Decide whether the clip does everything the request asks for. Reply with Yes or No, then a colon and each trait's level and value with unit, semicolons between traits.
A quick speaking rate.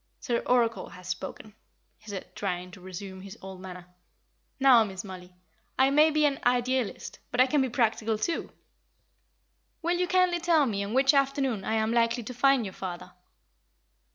No: average, 175 wpm